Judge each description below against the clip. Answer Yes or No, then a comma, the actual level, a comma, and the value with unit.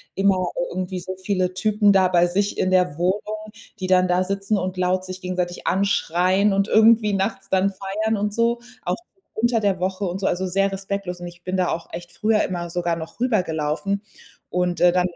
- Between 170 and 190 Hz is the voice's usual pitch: Yes, medium, 185 Hz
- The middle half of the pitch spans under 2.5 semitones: Yes, narrow, 1.9 semitones